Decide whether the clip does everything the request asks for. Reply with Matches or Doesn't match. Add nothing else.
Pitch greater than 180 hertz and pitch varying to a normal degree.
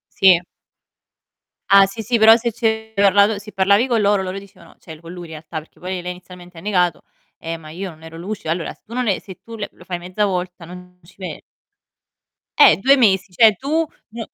Matches